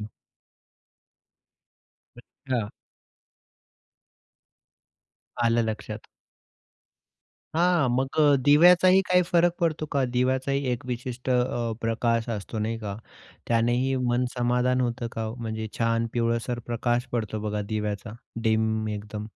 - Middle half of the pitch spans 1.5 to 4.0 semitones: Yes, average, 2.7 semitones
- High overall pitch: No, low, 120 Hz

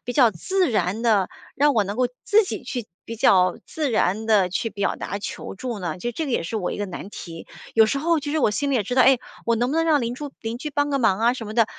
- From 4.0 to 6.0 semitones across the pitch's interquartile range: Yes, average, 5.2 semitones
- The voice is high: Yes, high, 235 Hz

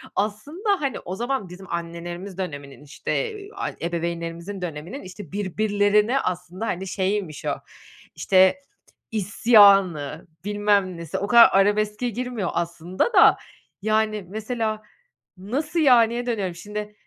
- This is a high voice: Yes, high, 205 Hz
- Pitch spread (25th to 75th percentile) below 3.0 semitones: No, average, 3.8 semitones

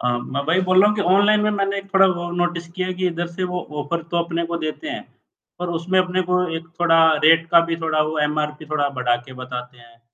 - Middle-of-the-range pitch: Yes, medium, 170 Hz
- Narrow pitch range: No, average, 3.3 semitones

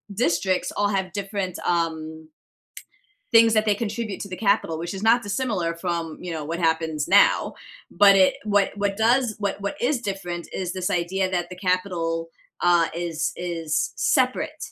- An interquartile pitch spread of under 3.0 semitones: No, average, 3.3 semitones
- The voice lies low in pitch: No, medium, 185 Hz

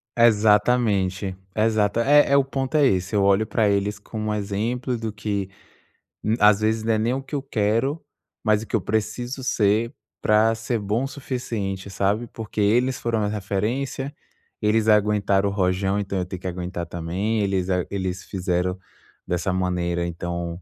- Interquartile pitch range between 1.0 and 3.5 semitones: Yes, average, 3.0 semitones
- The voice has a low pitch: Yes, low, 105 Hz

